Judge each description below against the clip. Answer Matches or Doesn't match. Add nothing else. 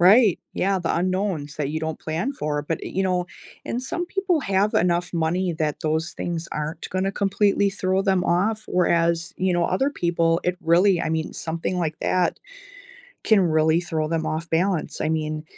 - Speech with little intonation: Doesn't match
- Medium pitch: Matches